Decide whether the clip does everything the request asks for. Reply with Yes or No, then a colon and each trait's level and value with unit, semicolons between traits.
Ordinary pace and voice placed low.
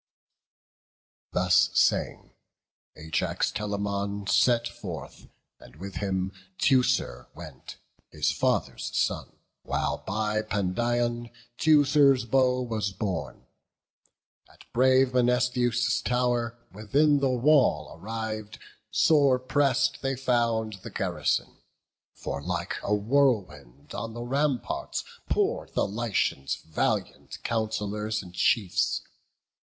No: slow, 100 wpm; low, 110 Hz